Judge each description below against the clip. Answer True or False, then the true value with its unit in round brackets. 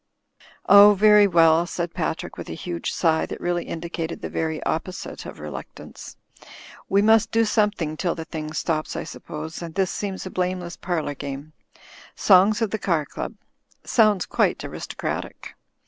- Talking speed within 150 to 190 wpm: True (160 wpm)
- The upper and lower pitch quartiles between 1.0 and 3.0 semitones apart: False (4.1 semitones)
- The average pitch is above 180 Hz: False (175 Hz)